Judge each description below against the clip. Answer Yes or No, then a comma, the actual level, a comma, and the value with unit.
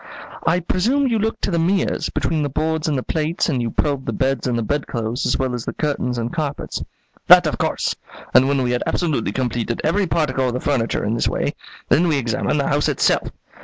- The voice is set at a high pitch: No, medium, 140 Hz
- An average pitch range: Yes, average, 4.7 semitones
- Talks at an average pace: No, fast, 225 wpm